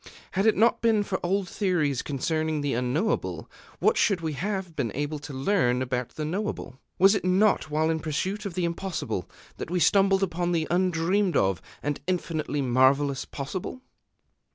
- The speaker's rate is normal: Yes, average, 170 wpm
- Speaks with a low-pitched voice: No, medium, 165 Hz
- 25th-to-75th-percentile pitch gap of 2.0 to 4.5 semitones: No, average, 5.1 semitones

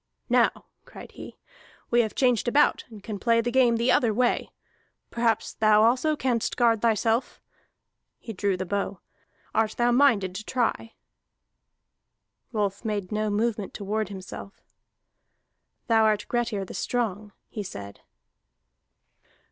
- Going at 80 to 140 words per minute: Yes, slow, 135 wpm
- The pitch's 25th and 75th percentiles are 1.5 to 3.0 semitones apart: Yes, average, 2.7 semitones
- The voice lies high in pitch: Yes, high, 220 Hz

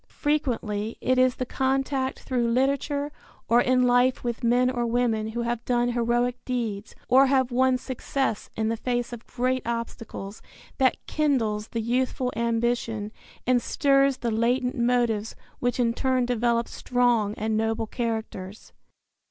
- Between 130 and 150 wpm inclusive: Yes, average, 145 wpm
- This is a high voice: Yes, high, 245 Hz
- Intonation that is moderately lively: No, narrow, 2.0 semitones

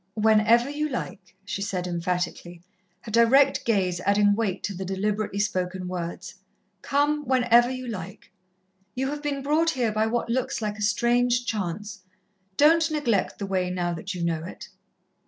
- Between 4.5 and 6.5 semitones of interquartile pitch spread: Yes, average, 5.0 semitones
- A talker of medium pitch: No, high, 215 Hz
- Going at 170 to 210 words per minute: No, average, 160 wpm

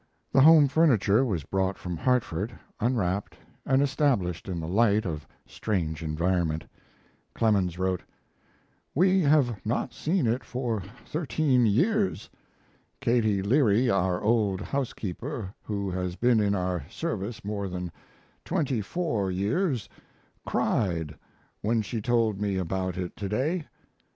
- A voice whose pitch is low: Yes, low, 105 Hz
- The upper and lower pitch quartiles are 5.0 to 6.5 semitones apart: Yes, wide, 5.5 semitones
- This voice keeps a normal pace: No, slow, 125 wpm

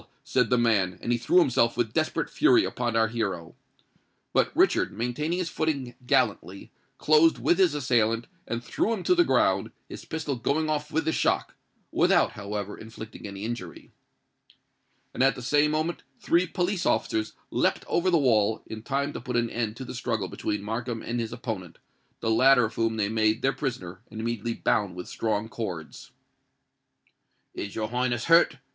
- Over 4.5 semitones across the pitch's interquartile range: Yes, average, 5.1 semitones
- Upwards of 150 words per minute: Yes, average, 175 wpm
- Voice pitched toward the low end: Yes, low, 120 Hz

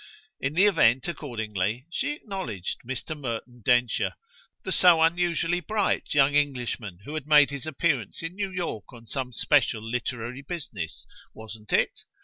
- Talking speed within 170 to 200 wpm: No, average, 145 wpm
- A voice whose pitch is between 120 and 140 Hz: Yes, low, 135 Hz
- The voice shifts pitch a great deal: Yes, wide, 6.4 semitones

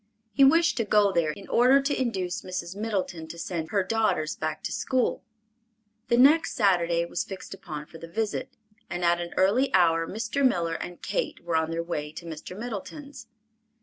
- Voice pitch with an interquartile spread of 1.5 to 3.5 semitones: No, average, 5.3 semitones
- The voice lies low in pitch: No, medium, 185 Hz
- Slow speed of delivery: No, average, 185 wpm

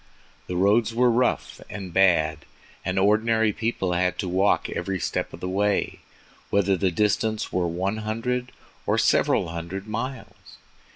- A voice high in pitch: No, low, 100 Hz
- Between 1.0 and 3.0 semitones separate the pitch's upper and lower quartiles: No, average, 3.4 semitones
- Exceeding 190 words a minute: No, average, 150 wpm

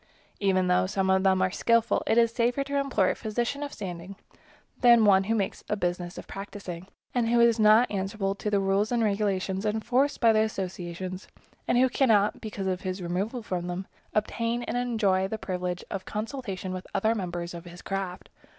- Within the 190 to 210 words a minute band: Yes, average, 200 wpm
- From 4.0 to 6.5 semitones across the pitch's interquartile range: No, average, 3.6 semitones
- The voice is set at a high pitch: Yes, high, 200 Hz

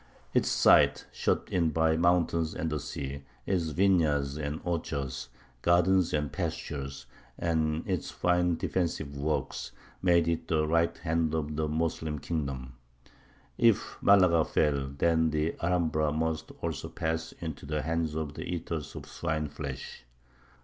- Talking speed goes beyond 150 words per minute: No, slow, 135 wpm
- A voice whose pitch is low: Yes, very low, 80 Hz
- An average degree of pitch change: No, narrow, 2.0 semitones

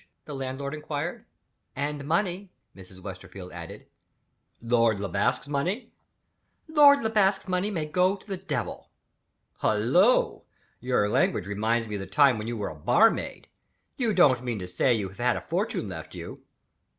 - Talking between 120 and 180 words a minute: Yes, average, 160 wpm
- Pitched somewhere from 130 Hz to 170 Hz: Yes, low, 135 Hz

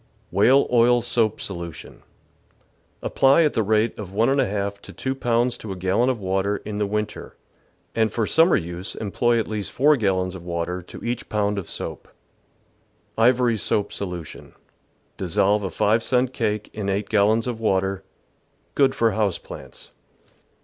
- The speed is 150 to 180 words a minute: Yes, average, 165 wpm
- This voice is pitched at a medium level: No, low, 105 Hz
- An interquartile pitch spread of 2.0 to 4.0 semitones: Yes, average, 3.5 semitones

